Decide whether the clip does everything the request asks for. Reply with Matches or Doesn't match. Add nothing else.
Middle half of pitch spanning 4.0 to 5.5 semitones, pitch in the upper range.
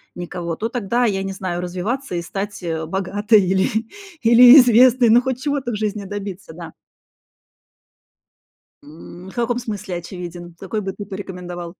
Matches